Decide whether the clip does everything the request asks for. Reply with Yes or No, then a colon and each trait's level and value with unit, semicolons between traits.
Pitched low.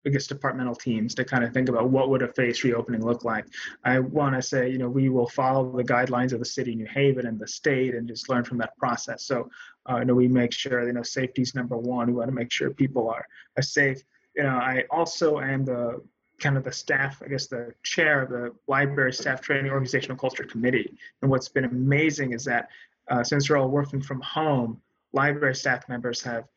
Yes: low, 130 Hz